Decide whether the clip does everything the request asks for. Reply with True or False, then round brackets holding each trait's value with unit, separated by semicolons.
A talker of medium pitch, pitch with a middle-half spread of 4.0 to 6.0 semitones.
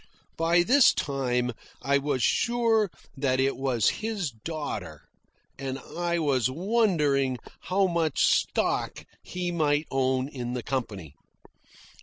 True (145 Hz; 5.1 semitones)